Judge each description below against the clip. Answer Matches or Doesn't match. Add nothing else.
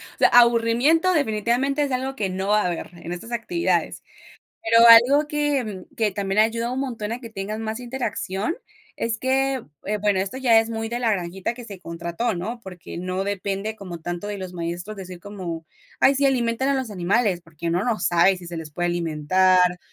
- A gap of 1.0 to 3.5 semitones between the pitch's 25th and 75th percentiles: Doesn't match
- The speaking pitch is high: Matches